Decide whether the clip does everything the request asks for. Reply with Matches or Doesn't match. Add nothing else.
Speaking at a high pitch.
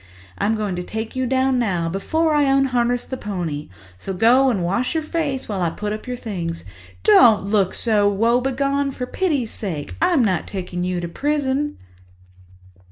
Matches